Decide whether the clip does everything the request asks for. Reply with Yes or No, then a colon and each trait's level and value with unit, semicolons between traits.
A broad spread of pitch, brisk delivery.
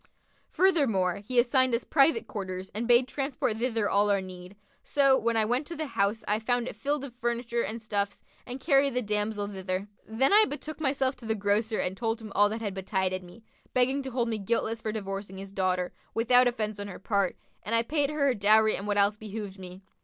No: average, 4.0 semitones; fast, 220 wpm